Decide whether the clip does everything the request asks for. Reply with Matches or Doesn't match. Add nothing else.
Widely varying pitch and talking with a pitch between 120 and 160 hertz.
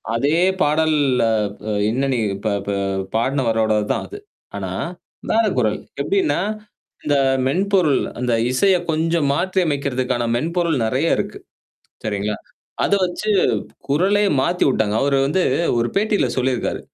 Matches